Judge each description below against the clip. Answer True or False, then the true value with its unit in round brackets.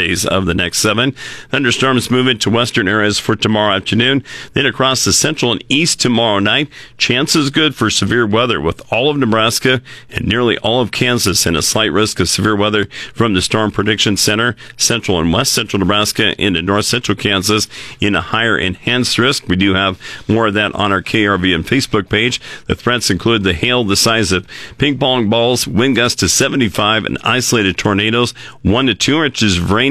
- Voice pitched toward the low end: True (110 Hz)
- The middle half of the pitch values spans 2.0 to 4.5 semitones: True (3.7 semitones)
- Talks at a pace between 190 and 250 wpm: True (195 wpm)